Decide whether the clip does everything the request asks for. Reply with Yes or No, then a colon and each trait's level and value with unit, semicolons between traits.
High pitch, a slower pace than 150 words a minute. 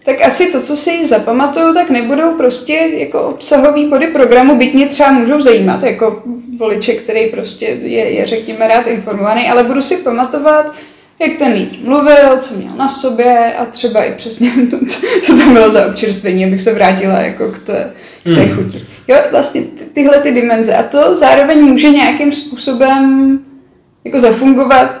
No: very high, 265 Hz; fast, 170 wpm